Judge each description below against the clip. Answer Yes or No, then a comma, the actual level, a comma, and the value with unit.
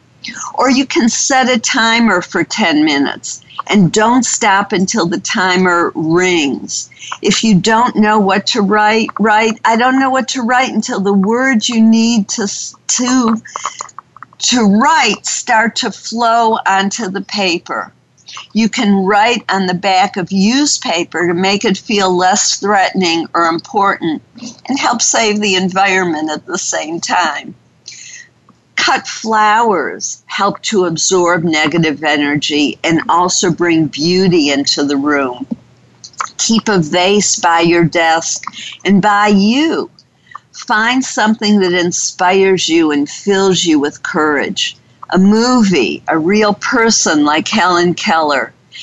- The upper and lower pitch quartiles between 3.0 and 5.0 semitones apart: Yes, average, 4.3 semitones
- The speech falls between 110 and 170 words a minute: Yes, average, 140 wpm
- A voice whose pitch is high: Yes, high, 200 Hz